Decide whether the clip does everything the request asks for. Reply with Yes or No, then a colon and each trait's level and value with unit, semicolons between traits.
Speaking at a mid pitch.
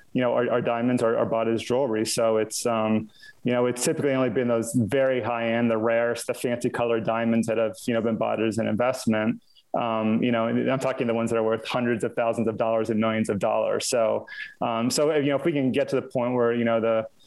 No: low, 115 Hz